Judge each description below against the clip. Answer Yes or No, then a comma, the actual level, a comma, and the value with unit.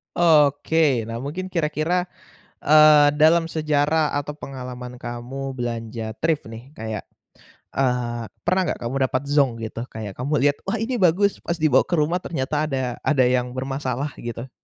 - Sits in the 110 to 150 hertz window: Yes, medium, 140 Hz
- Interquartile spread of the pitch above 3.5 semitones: Yes, average, 4.0 semitones